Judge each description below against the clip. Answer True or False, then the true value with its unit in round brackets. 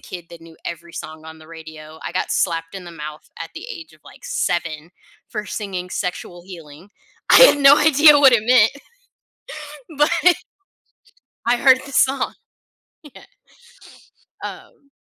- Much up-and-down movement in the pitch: True (8.5 semitones)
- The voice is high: False (180 Hz)